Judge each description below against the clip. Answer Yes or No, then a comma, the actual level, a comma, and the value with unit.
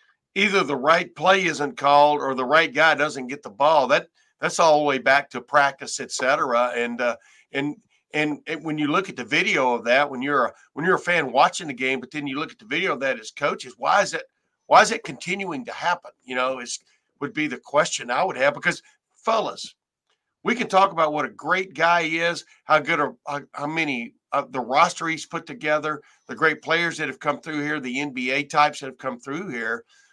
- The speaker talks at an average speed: No, fast, 235 wpm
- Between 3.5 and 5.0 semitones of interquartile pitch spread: No, average, 3.1 semitones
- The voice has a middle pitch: Yes, medium, 150 Hz